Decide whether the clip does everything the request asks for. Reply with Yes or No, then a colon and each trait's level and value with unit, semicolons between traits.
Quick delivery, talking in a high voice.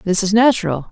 No: average, 195 wpm; high, 200 Hz